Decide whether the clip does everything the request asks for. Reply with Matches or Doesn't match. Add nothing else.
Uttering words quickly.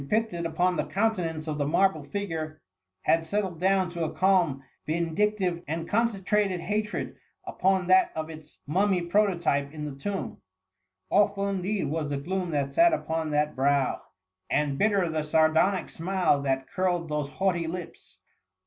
Doesn't match